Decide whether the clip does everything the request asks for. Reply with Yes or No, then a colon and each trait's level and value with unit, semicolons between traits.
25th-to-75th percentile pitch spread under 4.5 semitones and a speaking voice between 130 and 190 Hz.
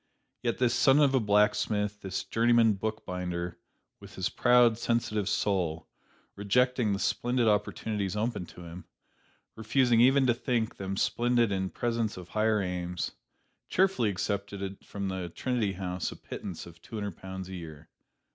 No: average, 3.9 semitones; low, 105 Hz